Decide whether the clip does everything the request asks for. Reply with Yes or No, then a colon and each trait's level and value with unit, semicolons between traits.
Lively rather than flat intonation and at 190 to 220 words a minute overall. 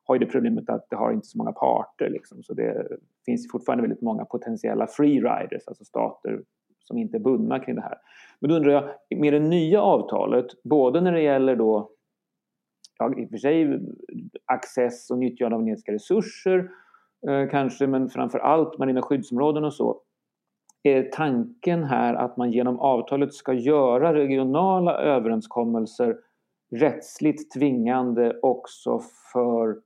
No: wide, 6.8 semitones; average, 155 wpm